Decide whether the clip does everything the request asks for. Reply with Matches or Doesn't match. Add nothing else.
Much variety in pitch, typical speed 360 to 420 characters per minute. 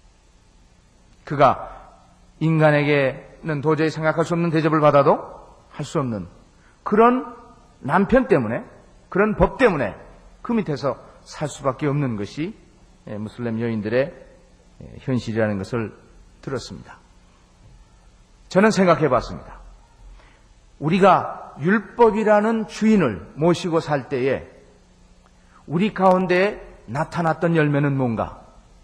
Doesn't match